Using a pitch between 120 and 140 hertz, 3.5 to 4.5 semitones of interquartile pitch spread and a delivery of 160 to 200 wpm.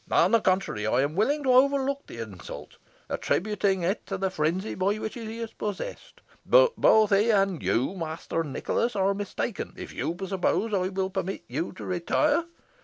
No: high, 195 Hz; average, 4.2 semitones; average, 180 wpm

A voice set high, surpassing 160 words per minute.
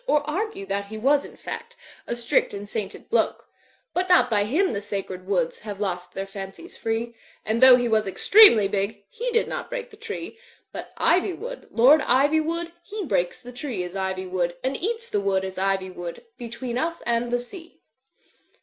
Yes: high, 235 Hz; average, 190 wpm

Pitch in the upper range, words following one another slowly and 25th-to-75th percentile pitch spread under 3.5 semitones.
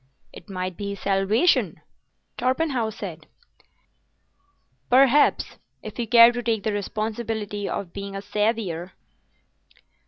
Yes: high, 215 Hz; slow, 105 wpm; average, 3.1 semitones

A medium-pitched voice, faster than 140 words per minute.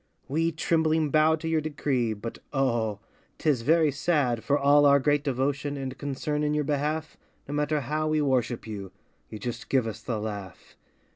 Yes: medium, 145 Hz; average, 180 wpm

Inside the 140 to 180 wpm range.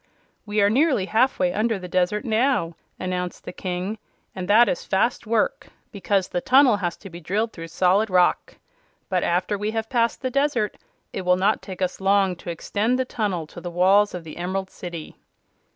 No: average, 190 wpm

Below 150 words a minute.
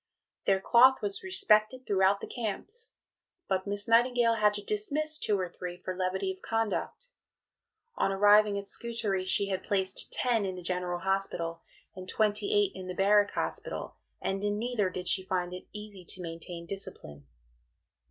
No: average, 165 wpm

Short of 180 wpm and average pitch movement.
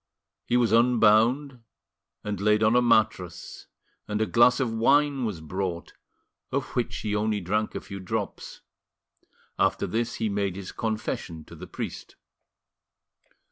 Yes: average, 140 wpm; average, 3.0 semitones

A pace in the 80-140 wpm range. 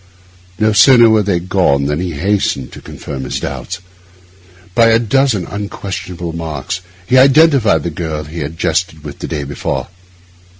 No: average, 160 wpm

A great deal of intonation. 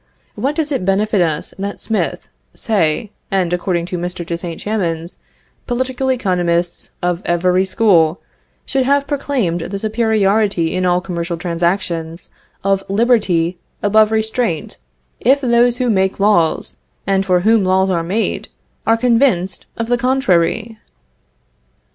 No: average, 4.6 semitones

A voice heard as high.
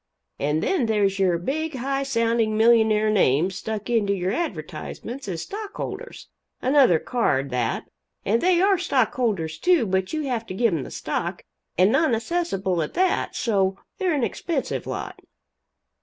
Yes: high, 225 Hz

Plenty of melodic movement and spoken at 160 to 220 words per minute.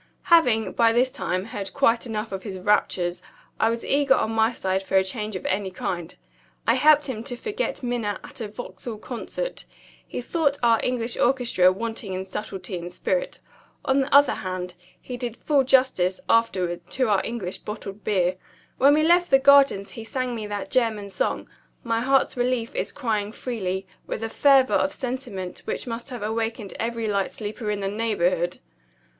No: average, 4.6 semitones; average, 180 wpm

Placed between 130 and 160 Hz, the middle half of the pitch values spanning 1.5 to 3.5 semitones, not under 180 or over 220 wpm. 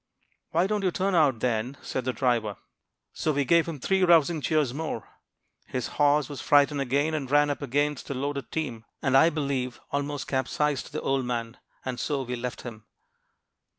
Yes: medium, 140 Hz; average, 3.2 semitones; average, 185 wpm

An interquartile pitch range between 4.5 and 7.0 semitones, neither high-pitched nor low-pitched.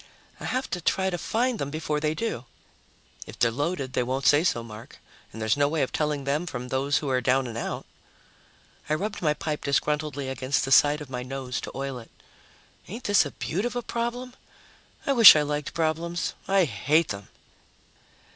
Yes: average, 4.8 semitones; medium, 150 Hz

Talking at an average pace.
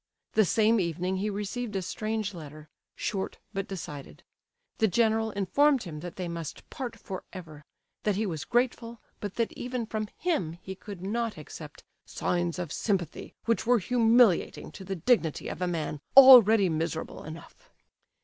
Yes: average, 160 wpm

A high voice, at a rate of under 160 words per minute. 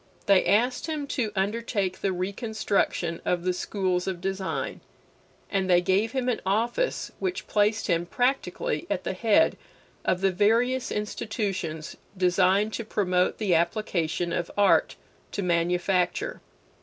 Yes: high, 195 Hz; slow, 135 wpm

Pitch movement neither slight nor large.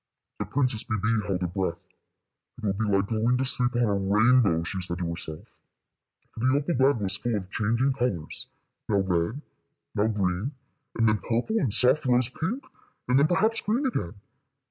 Yes: average, 4.8 semitones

